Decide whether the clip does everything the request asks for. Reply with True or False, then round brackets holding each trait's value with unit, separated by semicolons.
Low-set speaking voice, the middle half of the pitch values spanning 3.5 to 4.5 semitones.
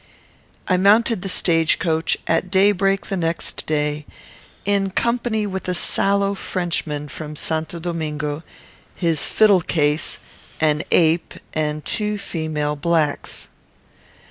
False (170 Hz; 4.2 semitones)